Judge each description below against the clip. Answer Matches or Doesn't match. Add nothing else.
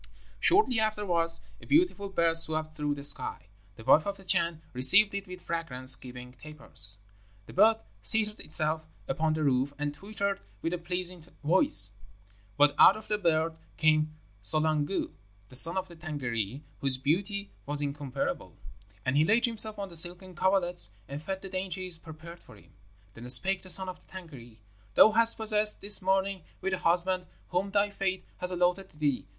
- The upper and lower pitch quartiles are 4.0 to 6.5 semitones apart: Matches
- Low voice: Doesn't match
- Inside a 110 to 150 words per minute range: Doesn't match